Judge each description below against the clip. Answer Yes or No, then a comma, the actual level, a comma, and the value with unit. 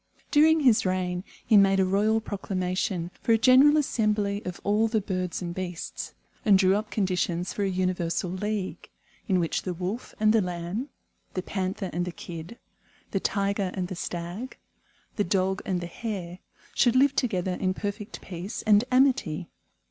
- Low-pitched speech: No, high, 195 Hz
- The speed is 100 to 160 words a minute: No, average, 170 wpm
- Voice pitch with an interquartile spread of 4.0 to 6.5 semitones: No, average, 3.0 semitones